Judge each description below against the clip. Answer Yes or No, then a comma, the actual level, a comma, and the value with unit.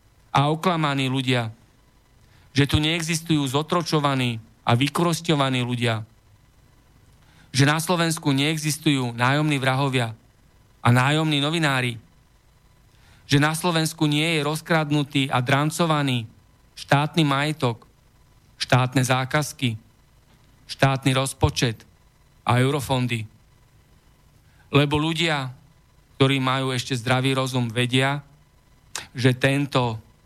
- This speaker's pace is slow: Yes, slow, 90 wpm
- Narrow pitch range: No, average, 3.1 semitones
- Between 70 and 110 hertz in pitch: No, low, 135 Hz